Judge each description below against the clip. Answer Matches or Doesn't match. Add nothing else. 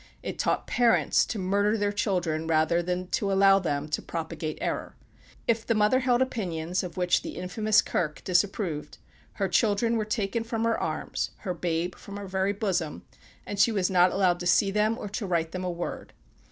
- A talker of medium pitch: Doesn't match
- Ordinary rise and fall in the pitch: Matches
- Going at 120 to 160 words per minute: Doesn't match